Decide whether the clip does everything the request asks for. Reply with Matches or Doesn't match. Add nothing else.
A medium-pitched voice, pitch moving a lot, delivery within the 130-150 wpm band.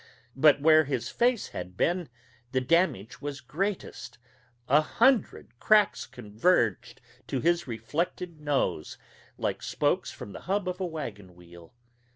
Matches